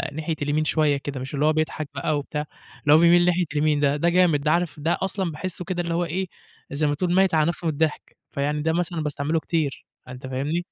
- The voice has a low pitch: No, medium, 155 Hz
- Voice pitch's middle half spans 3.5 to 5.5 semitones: No, average, 2.8 semitones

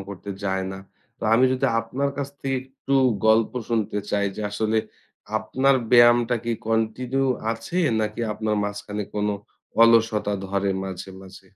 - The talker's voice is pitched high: No, low, 110 Hz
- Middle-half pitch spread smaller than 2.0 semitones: No, average, 2.9 semitones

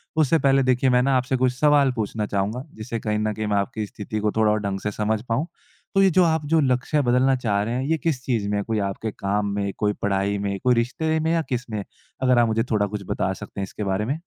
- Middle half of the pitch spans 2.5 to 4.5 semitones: Yes, average, 4.2 semitones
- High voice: No, low, 115 Hz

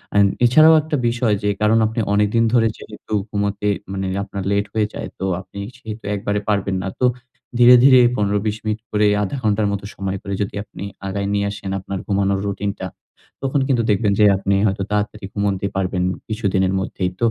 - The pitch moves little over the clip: Yes, narrow, 1.8 semitones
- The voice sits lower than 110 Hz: Yes, low, 100 Hz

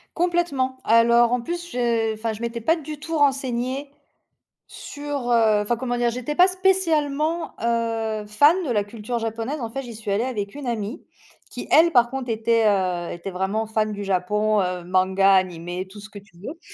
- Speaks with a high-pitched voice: Yes, high, 230 Hz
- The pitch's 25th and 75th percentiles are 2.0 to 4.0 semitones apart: No, average, 4.8 semitones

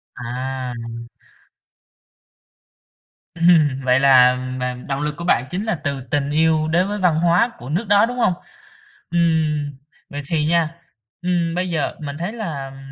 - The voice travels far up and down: No, average, 4.3 semitones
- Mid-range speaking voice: Yes, medium, 155 Hz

